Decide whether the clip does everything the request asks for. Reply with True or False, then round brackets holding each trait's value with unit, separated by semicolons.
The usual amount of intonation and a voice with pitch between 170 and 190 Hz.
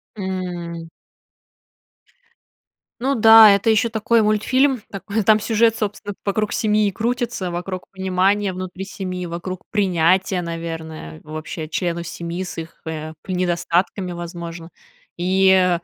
True (3.5 semitones; 185 Hz)